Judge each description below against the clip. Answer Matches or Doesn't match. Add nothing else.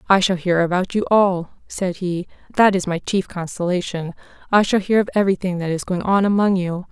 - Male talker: Doesn't match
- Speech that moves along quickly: Matches